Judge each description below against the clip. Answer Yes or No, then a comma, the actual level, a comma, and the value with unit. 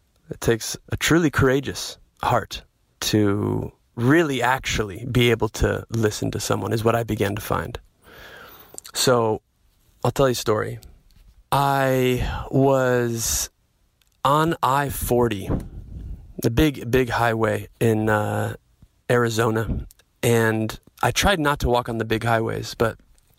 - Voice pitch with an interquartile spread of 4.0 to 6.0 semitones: No, average, 3.4 semitones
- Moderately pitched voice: No, low, 115 Hz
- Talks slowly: Yes, slow, 130 wpm